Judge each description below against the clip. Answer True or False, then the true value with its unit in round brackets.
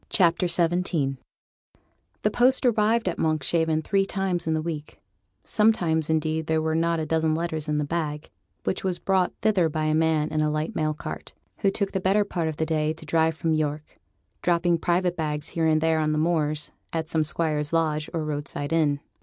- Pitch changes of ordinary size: False (2.1 semitones)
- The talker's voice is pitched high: False (160 Hz)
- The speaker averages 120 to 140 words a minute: False (205 wpm)